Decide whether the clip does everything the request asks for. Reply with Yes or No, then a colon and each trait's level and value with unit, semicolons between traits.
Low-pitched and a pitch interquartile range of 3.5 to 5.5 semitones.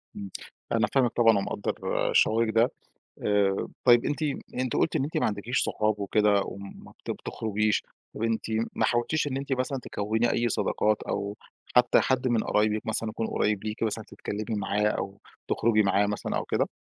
No: low, 110 Hz; narrow, 2.6 semitones